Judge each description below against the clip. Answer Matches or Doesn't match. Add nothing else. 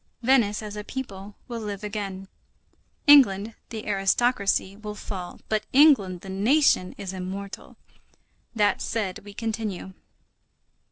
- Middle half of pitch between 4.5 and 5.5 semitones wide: Doesn't match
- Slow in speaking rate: Matches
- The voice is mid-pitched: Doesn't match